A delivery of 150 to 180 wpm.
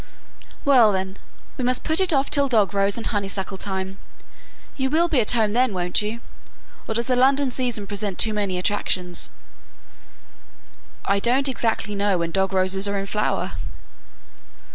Yes: average, 165 wpm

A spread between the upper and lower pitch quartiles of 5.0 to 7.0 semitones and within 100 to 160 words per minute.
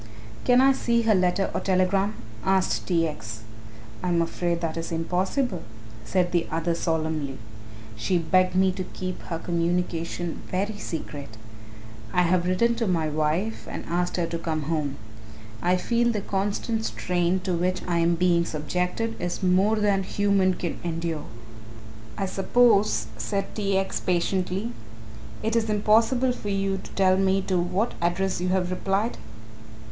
No: average, 2.8 semitones; average, 155 wpm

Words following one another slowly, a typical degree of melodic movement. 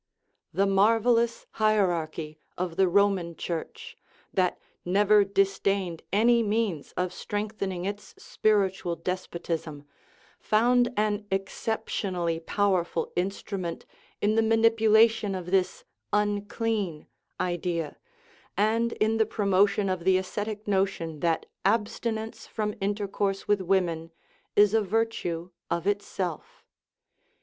Yes: slow, 115 wpm; average, 3.2 semitones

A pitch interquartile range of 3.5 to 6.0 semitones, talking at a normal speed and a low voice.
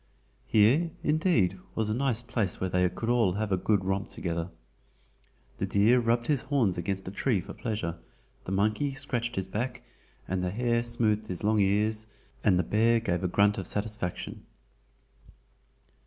Yes: average, 3.8 semitones; average, 165 wpm; low, 105 Hz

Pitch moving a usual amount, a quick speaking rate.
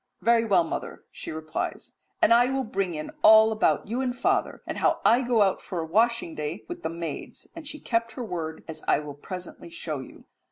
No: wide, 6.4 semitones; fast, 215 wpm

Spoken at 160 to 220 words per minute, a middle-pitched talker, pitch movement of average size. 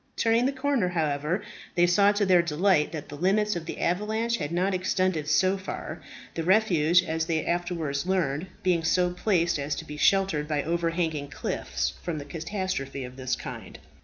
Yes: average, 180 wpm; medium, 175 Hz; average, 3.9 semitones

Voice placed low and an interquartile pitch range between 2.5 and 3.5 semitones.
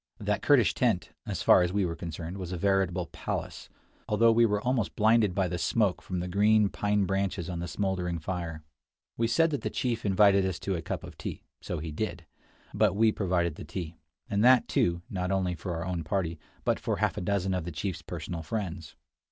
Yes: very low, 95 Hz; average, 3.1 semitones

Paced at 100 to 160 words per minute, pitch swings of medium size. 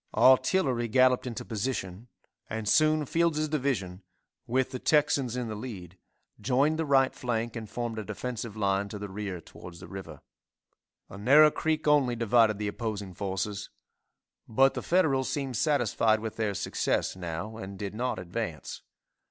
Yes: average, 155 wpm; average, 4.6 semitones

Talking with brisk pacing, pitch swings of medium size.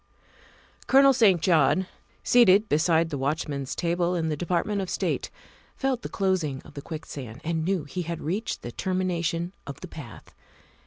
No: average, 165 wpm; average, 3.8 semitones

